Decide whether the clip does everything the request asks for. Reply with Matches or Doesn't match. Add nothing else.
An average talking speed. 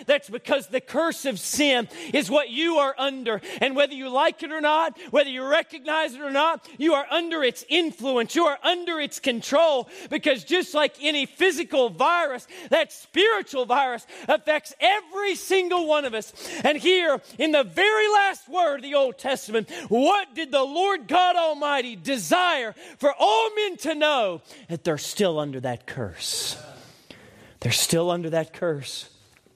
Matches